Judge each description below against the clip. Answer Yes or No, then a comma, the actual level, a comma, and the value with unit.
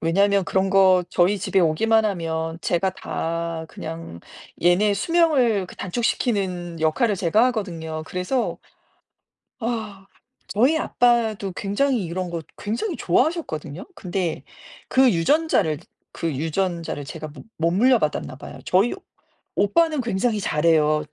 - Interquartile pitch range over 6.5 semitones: No, average, 5.3 semitones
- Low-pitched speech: No, high, 190 Hz